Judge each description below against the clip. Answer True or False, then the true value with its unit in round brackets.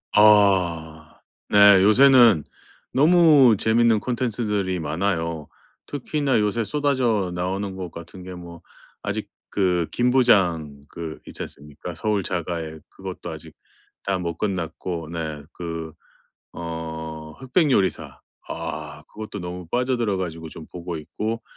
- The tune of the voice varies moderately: True (4.9 semitones)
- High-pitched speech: False (90 Hz)